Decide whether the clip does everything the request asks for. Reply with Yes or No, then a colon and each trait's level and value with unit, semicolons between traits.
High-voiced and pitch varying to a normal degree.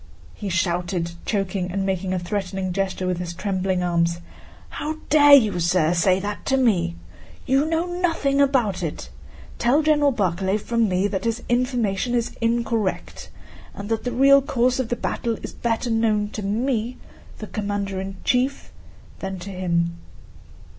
Yes: high, 205 Hz; average, 4.8 semitones